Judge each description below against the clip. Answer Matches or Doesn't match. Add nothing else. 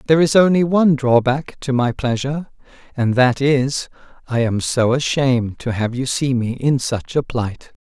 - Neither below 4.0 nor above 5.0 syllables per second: Matches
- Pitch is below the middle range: Matches